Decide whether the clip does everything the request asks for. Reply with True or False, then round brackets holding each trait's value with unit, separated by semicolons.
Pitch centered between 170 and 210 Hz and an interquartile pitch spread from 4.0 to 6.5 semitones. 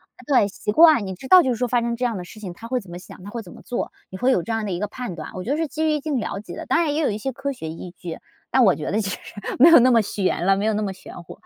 False (220 Hz; 5.4 semitones)